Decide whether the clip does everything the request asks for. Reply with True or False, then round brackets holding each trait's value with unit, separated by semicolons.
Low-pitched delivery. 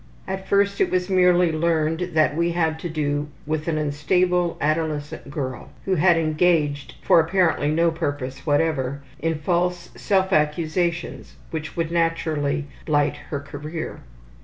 False (160 Hz)